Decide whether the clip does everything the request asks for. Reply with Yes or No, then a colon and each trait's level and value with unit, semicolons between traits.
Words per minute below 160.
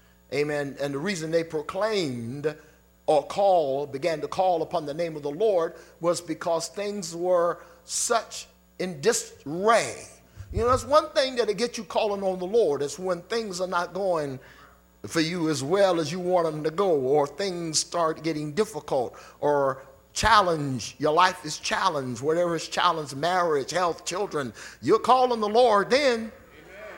No: average, 165 wpm